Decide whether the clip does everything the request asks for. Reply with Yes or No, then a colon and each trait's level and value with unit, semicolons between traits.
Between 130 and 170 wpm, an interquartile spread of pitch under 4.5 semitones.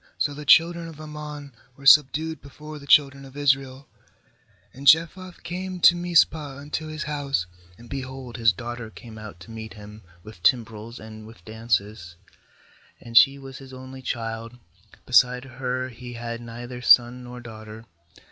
Yes: average, 155 wpm; average, 4.0 semitones